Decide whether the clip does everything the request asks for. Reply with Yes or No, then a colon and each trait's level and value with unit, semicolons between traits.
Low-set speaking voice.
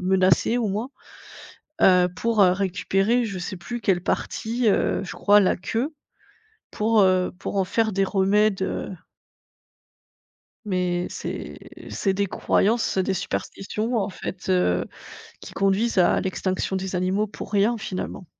No: high, 195 Hz